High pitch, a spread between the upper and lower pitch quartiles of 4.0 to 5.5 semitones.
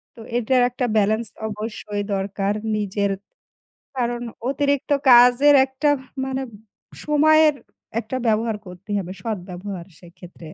Yes: high, 220 Hz; average, 4.7 semitones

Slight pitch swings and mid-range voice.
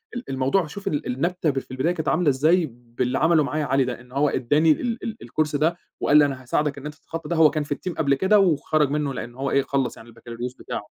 No: average, 3.6 semitones; medium, 145 Hz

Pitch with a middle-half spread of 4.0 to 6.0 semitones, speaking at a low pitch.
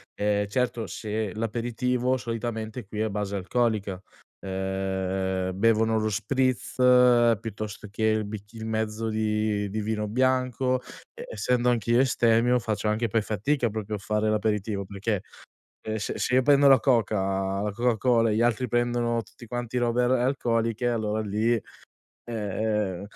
No: narrow, 2.5 semitones; low, 110 Hz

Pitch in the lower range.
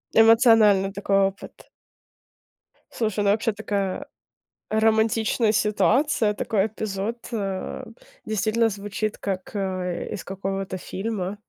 No: high, 210 Hz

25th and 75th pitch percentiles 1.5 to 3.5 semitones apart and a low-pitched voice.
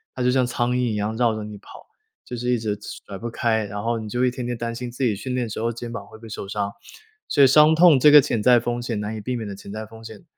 Yes: narrow, 2.5 semitones; low, 115 Hz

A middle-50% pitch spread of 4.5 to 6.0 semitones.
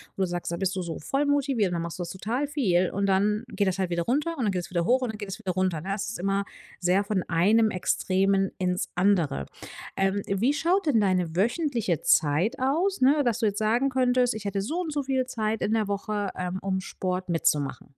Yes: average, 5.2 semitones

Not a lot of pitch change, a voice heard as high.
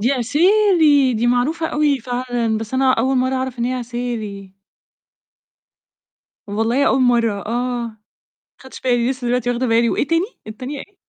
Yes: narrow, 2.3 semitones; very high, 250 Hz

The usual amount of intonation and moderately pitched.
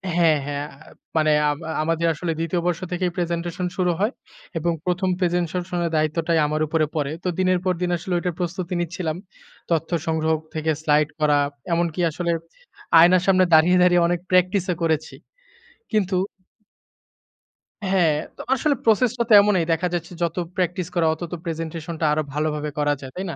No: narrow, 2.3 semitones; medium, 170 Hz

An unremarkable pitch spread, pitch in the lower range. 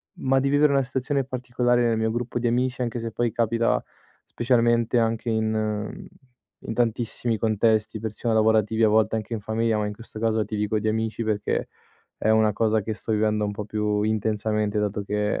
No: narrow, 1.7 semitones; low, 110 Hz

